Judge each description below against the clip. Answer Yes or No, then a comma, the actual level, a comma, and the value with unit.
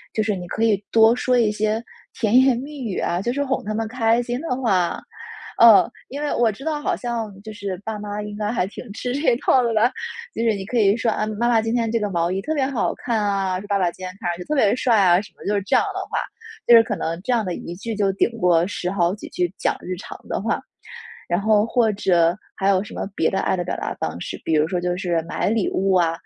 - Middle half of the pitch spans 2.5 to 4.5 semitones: Yes, average, 3.8 semitones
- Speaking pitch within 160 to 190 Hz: No, high, 210 Hz